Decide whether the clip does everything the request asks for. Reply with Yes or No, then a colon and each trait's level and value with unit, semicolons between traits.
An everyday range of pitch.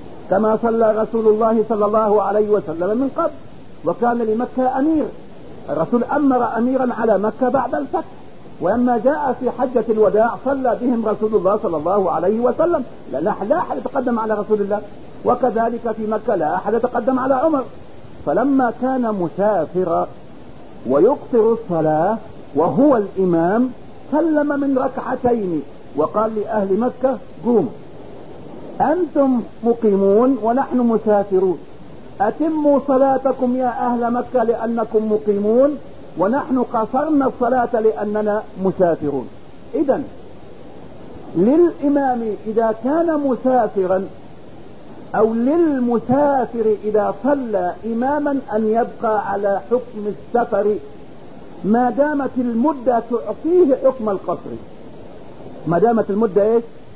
Yes: average, 3.7 semitones